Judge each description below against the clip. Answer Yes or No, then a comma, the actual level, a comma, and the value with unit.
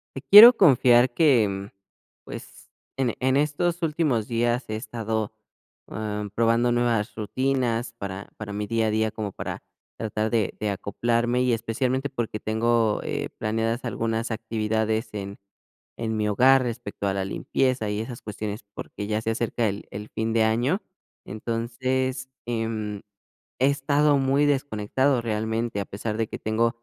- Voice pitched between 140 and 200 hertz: No, low, 115 Hz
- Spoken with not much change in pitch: No, average, 3.0 semitones